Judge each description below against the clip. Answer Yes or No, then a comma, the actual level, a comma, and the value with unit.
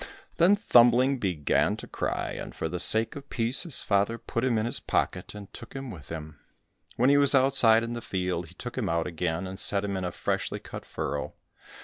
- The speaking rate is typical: No, fast, 220 wpm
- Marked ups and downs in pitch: Yes, wide, 6.0 semitones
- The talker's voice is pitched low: Yes, low, 110 Hz